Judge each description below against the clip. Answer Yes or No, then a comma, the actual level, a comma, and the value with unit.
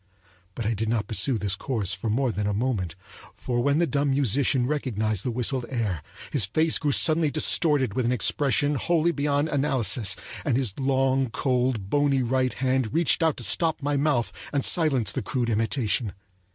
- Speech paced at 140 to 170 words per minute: No, average, 180 wpm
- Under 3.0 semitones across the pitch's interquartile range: No, average, 4.2 semitones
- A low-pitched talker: Yes, low, 130 Hz